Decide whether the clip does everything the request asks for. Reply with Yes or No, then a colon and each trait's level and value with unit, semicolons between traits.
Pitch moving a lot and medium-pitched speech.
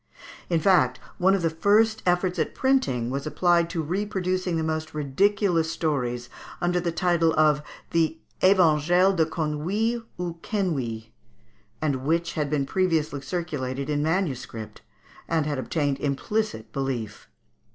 No: average, 4.2 semitones; medium, 160 Hz